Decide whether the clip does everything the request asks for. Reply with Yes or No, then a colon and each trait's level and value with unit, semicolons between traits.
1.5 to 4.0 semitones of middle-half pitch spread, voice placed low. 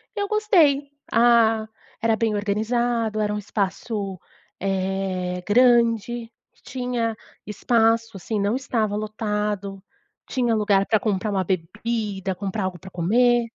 No: average, 3.1 semitones; high, 215 Hz